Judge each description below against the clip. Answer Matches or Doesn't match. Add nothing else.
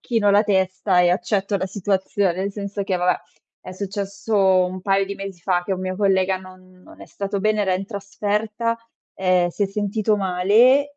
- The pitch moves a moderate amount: Doesn't match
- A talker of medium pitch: Doesn't match